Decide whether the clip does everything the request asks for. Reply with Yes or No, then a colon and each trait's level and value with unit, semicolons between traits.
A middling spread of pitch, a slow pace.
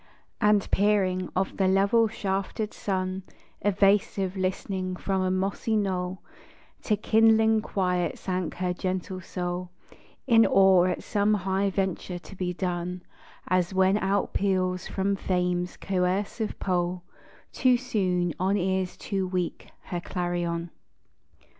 No: narrow, 1.7 semitones; slow, 120 wpm